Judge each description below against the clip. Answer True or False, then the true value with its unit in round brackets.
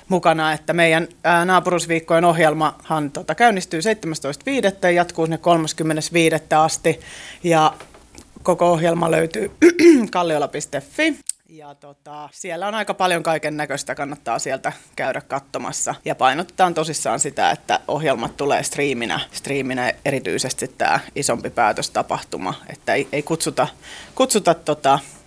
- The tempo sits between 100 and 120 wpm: True (115 wpm)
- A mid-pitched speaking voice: True (165 Hz)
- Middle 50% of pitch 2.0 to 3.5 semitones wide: True (2.8 semitones)